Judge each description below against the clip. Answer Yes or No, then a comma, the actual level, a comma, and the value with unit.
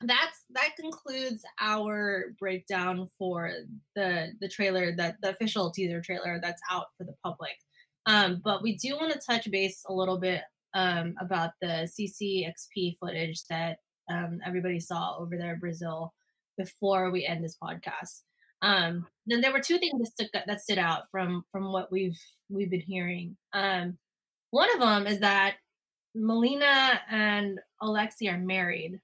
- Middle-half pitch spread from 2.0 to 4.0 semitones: Yes, average, 3.3 semitones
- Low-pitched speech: No, high, 190 Hz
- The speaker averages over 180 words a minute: No, average, 155 wpm